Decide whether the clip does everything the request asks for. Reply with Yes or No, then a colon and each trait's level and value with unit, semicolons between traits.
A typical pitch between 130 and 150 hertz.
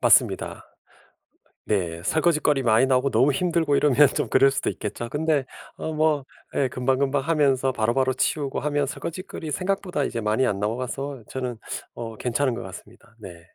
Yes: low, 135 Hz